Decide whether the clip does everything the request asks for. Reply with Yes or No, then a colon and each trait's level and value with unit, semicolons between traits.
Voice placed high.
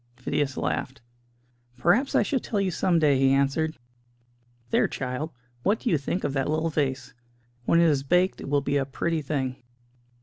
No: medium, 145 Hz